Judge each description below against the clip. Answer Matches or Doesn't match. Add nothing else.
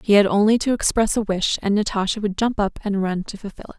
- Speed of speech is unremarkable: Doesn't match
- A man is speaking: Doesn't match